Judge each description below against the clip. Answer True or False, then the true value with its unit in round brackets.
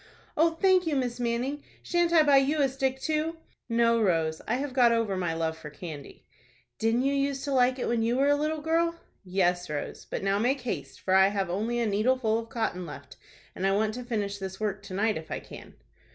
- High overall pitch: True (230 Hz)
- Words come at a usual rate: False (225 wpm)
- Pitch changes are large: True (6.1 semitones)